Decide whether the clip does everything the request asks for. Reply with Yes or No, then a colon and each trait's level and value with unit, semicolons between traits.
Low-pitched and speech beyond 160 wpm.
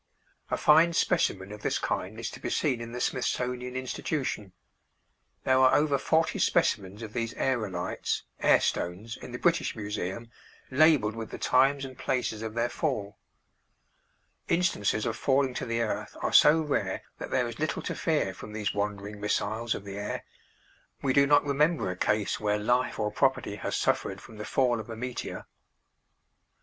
Yes: low, 115 Hz; average, 175 wpm